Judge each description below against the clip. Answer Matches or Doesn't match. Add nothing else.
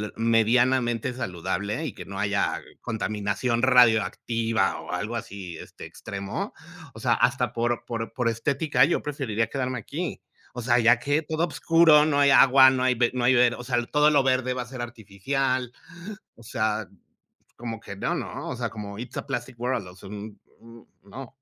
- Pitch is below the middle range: Matches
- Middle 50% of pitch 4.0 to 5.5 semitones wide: Doesn't match